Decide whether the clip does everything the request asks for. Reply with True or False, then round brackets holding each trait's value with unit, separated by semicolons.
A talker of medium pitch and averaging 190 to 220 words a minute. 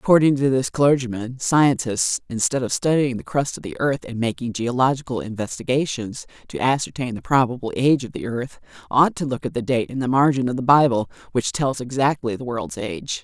False (130 Hz; 195 wpm)